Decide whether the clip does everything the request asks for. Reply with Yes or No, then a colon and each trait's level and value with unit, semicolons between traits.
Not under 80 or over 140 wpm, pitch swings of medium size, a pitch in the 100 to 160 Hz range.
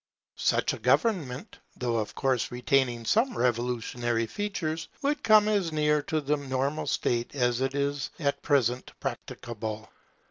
Yes: slow, 135 wpm; average, 4.3 semitones; low, 135 Hz